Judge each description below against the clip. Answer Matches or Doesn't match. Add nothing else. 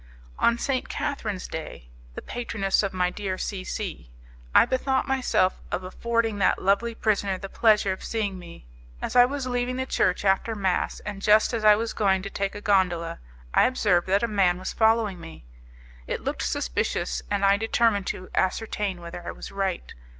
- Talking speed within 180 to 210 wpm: Matches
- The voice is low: Doesn't match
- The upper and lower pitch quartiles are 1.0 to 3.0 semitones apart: Doesn't match